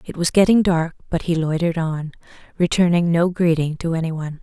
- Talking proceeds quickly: No, average, 190 wpm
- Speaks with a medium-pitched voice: Yes, medium, 170 Hz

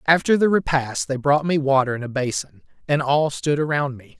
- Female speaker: No, male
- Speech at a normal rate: No, fast, 215 wpm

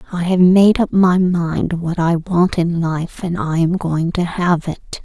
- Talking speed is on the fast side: Yes, fast, 215 wpm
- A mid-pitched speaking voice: Yes, medium, 175 Hz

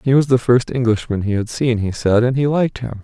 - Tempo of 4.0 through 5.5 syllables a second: No, 5.9 syllables/s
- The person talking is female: No, male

